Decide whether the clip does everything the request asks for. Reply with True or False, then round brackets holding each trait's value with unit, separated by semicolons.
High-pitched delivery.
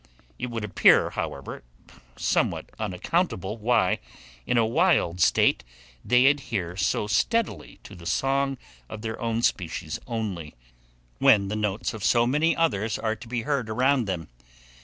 False (110 Hz)